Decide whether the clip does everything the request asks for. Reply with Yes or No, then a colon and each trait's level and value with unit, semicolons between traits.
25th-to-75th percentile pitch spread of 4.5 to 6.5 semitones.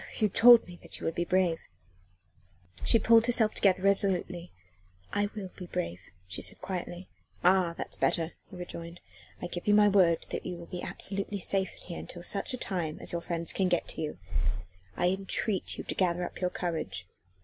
No: narrow, 2.4 semitones